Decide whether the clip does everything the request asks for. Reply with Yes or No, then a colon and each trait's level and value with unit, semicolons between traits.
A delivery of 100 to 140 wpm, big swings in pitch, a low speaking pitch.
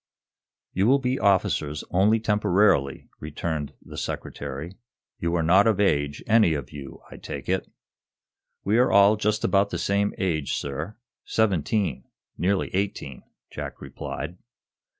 Yes: slow, 135 wpm; wide, 5.7 semitones; very low, 95 Hz